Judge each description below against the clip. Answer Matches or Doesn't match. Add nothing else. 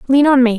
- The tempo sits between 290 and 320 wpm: Matches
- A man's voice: Doesn't match